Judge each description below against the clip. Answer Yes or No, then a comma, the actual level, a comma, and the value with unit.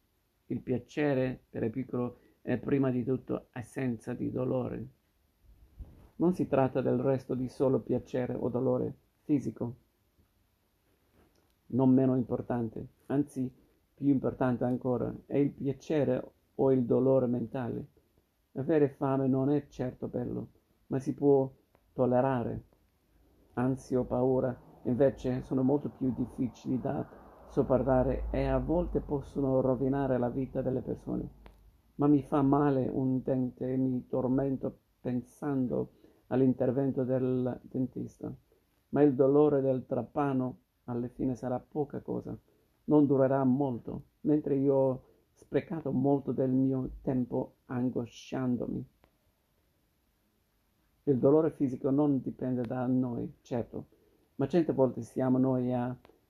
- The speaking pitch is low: Yes, low, 130 Hz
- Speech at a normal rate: Yes, average, 125 wpm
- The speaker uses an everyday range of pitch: No, narrow, 2.1 semitones